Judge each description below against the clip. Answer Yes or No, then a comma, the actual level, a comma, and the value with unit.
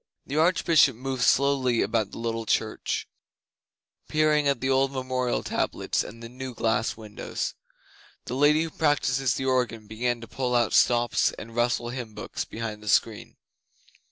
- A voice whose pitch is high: No, low, 125 Hz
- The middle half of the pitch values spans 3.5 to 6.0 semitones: No, average, 2.7 semitones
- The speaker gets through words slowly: No, average, 155 wpm